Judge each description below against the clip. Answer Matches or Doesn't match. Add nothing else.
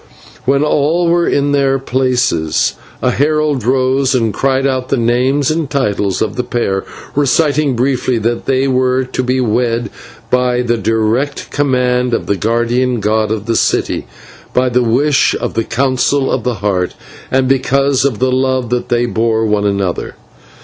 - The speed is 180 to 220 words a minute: Doesn't match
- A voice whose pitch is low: Matches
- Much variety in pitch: Doesn't match